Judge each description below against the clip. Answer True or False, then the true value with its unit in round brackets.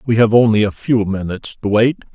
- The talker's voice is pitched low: True (110 Hz)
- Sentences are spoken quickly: True (225 wpm)